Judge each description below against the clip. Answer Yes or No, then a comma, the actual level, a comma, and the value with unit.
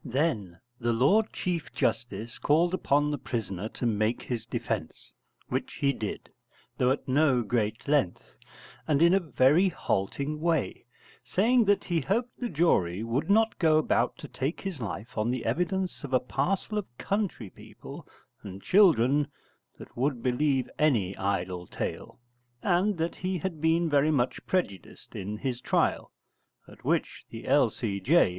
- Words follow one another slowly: No, average, 155 wpm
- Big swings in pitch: Yes, wide, 7.0 semitones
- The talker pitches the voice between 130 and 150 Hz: Yes, medium, 140 Hz